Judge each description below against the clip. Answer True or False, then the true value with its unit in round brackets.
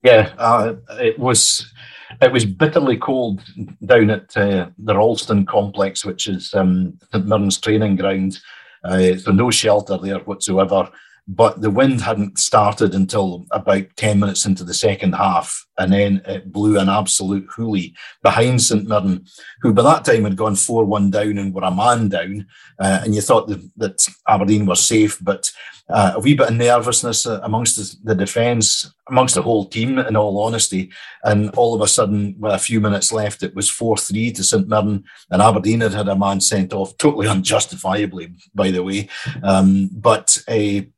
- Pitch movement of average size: False (2.3 semitones)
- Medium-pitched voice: False (100 Hz)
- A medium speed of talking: True (180 wpm)